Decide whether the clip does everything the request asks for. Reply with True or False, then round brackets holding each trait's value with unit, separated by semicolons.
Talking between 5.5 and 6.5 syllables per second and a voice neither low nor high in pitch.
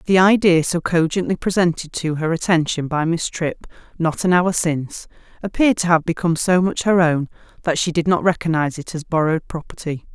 True (5.7 syllables/s; 170 Hz)